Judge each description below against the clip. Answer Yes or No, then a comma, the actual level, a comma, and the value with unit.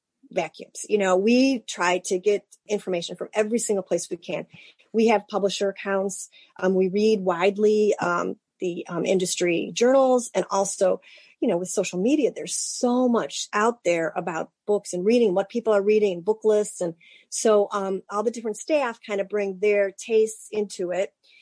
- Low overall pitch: No, high, 205 Hz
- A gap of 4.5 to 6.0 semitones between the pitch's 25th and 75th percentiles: No, average, 2.8 semitones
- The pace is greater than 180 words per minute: No, average, 175 wpm